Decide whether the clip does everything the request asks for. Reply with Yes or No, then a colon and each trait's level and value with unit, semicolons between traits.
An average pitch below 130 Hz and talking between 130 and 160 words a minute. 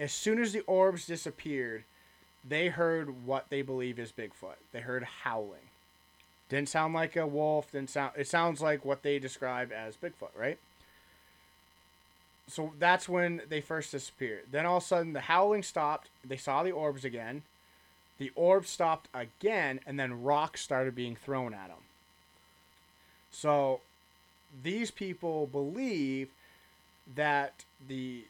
No: low, 135 Hz; average, 145 wpm